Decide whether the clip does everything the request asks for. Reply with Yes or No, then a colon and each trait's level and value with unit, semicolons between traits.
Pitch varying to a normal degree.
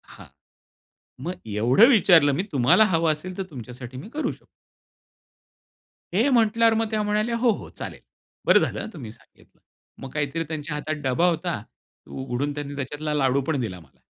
No: wide, 7.3 semitones